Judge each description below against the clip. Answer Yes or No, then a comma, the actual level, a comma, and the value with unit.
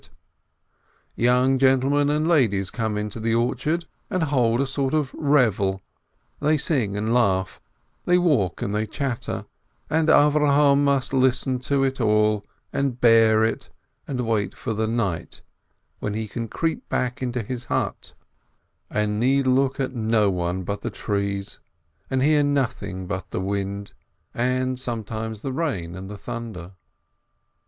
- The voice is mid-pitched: No, low, 120 Hz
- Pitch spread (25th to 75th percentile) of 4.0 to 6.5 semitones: Yes, average, 4.6 semitones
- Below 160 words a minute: Yes, average, 150 wpm